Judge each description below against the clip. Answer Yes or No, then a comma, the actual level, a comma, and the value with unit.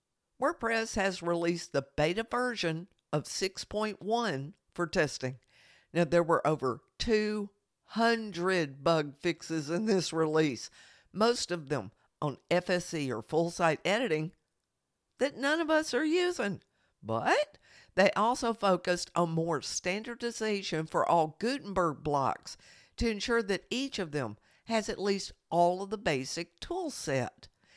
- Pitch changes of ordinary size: No, wide, 5.7 semitones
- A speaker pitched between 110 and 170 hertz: No, medium, 180 Hz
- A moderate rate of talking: No, slow, 130 wpm